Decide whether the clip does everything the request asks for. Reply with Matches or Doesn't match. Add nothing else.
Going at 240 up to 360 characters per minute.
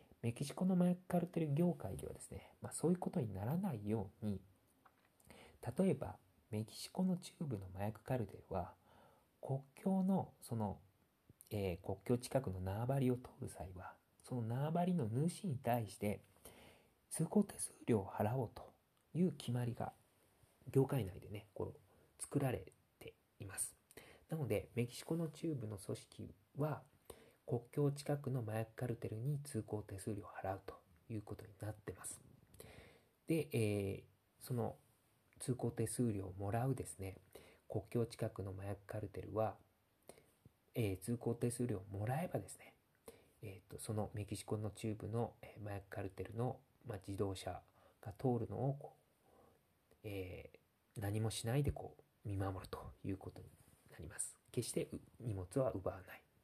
Matches